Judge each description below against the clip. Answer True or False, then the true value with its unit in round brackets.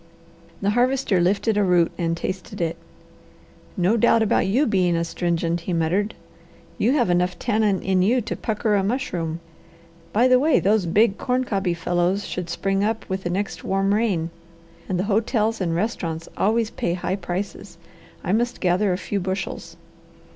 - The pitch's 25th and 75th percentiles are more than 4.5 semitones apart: False (3.8 semitones)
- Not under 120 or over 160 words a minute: False (170 wpm)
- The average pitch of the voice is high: True (195 Hz)